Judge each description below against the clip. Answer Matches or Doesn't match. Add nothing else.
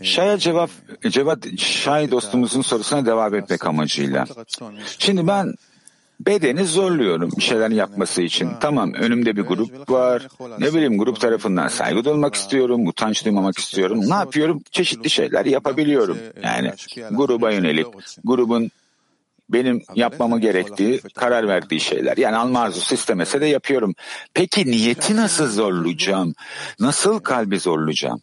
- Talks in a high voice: Doesn't match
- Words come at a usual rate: Matches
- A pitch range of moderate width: Doesn't match